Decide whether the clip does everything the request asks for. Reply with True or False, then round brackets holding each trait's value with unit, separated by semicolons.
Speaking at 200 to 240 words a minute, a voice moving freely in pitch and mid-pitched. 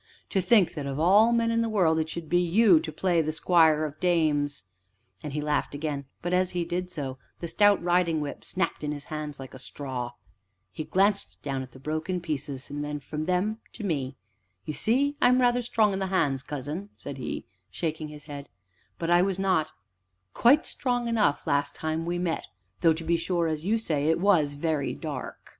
False (205 wpm; 4.2 semitones; 160 Hz)